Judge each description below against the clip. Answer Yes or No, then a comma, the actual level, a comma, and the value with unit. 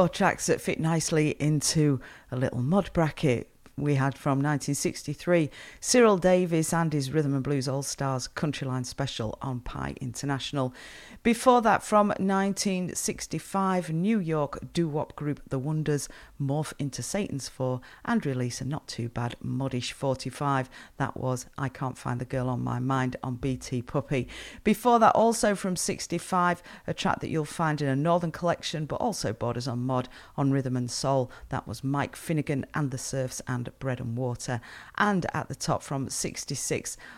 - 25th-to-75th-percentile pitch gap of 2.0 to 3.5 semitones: No, average, 4.7 semitones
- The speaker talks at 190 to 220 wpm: No, average, 165 wpm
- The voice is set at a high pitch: No, medium, 140 Hz